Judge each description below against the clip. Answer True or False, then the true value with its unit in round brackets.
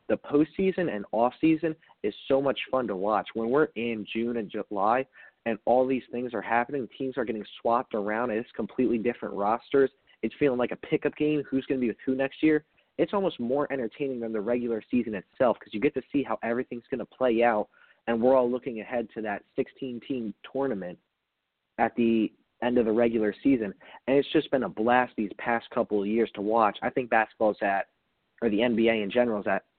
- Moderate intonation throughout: True (3.4 semitones)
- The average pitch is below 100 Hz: False (120 Hz)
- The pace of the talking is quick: True (210 wpm)